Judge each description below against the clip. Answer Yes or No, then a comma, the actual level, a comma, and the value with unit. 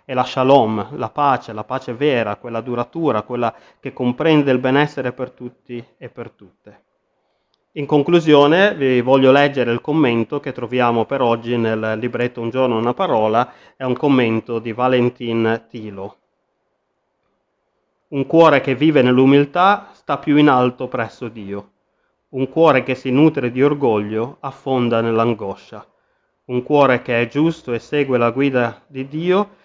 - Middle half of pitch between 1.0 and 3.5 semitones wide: Yes, average, 3.1 semitones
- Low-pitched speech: Yes, low, 125 Hz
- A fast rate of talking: No, average, 150 wpm